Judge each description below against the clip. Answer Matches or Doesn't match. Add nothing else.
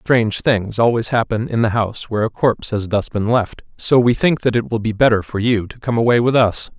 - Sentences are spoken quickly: Matches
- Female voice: Doesn't match